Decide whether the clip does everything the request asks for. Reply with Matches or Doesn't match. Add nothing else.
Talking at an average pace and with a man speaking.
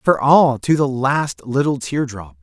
Matches